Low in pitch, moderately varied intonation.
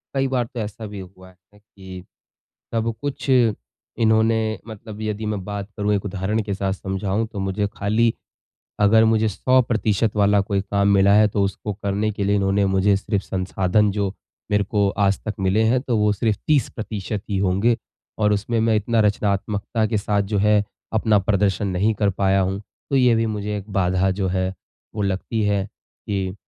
No: low, 105 Hz; narrow, 2.1 semitones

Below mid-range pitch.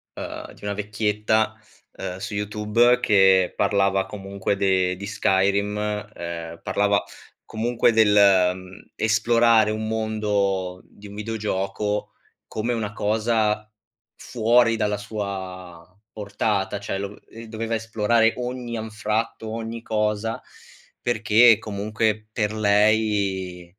Yes: low, 105 Hz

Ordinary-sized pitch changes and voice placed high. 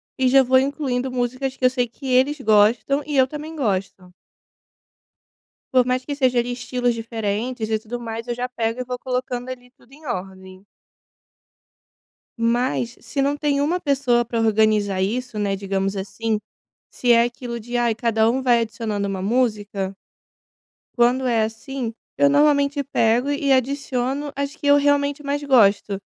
Yes: average, 3.3 semitones; high, 245 Hz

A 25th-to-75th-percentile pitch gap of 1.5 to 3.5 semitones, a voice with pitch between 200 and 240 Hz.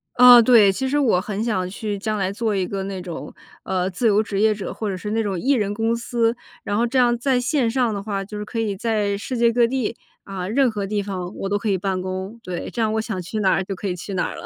Yes: average, 3.2 semitones; high, 210 Hz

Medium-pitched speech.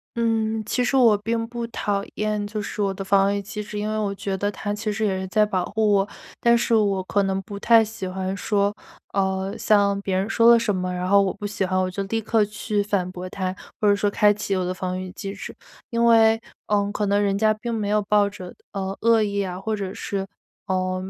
No: high, 205 Hz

